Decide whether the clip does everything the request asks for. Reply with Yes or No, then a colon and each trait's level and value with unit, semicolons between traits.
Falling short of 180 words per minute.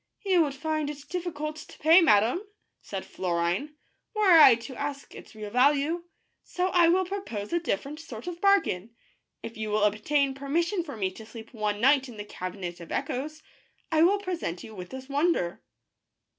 No: average, 185 wpm